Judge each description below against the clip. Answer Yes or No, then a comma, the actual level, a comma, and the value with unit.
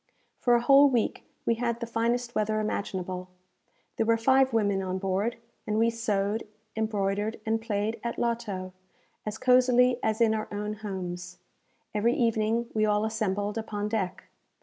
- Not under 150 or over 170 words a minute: Yes, average, 155 wpm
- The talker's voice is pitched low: No, high, 220 Hz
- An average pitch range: No, narrow, 2.3 semitones